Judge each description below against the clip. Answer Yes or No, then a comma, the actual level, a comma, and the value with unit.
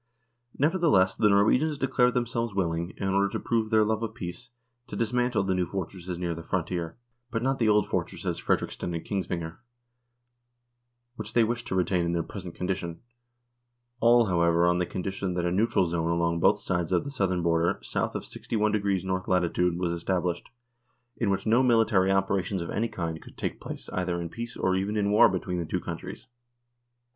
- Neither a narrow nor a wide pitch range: Yes, average, 4.1 semitones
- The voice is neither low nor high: No, very low, 95 Hz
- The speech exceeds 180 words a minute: Yes, average, 190 wpm